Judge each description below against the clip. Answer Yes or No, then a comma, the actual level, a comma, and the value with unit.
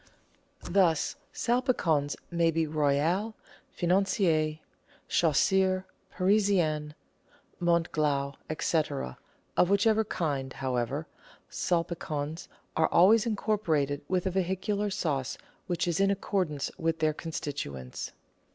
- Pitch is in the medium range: Yes, medium, 170 Hz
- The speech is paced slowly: Yes, slow, 95 wpm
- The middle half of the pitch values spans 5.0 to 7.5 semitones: No, average, 4.2 semitones